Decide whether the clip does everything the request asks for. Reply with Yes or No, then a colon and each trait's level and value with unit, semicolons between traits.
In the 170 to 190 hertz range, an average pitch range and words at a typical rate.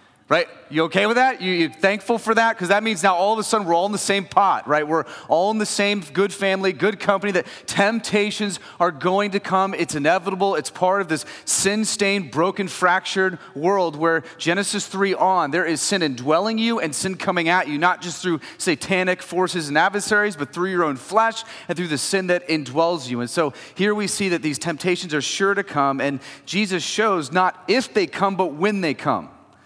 No: medium, 185 Hz; average, 3.2 semitones; fast, 215 wpm